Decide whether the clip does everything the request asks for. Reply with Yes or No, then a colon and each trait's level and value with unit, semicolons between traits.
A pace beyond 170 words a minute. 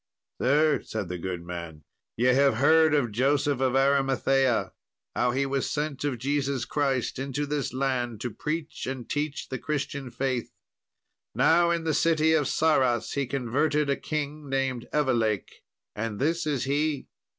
No: average, 155 wpm